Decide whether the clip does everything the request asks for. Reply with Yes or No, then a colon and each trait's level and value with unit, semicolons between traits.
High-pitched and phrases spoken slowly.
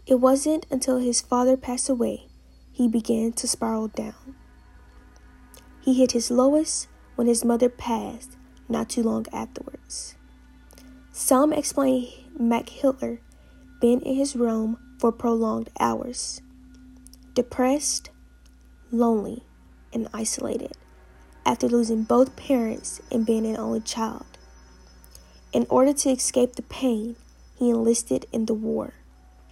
Yes: high, 235 Hz; slow, 120 wpm